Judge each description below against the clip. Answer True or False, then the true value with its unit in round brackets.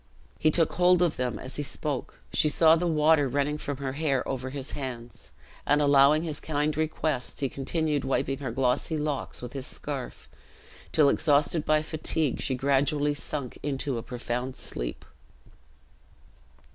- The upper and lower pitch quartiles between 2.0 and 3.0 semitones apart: True (2.6 semitones)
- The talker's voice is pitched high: False (145 Hz)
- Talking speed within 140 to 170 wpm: True (160 wpm)